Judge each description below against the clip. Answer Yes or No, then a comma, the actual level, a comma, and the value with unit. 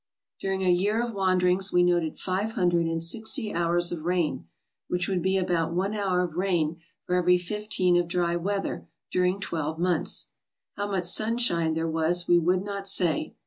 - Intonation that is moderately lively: No, narrow, 2.2 semitones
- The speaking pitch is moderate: Yes, medium, 180 Hz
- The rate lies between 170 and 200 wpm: Yes, average, 180 wpm